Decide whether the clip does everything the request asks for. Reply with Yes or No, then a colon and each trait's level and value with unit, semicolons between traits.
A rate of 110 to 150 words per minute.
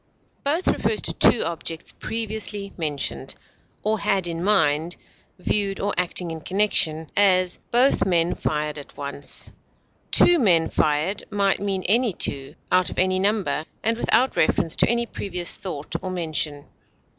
Yes: average, 145 wpm